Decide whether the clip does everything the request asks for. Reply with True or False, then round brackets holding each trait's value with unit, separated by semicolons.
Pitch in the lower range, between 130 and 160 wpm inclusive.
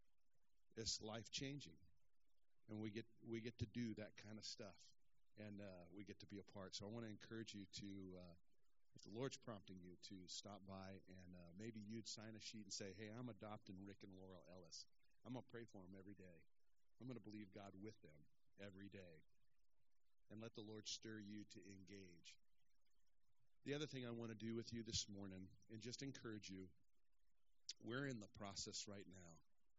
False (105 Hz; 200 wpm)